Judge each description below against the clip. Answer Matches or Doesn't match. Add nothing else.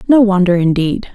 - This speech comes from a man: Doesn't match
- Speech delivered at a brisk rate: Doesn't match